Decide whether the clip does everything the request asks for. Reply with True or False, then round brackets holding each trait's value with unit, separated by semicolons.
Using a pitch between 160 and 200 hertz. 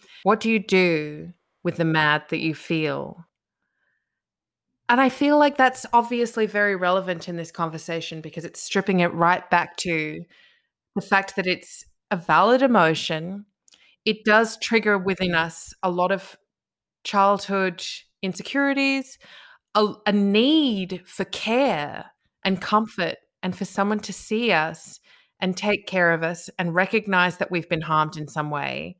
True (190 Hz)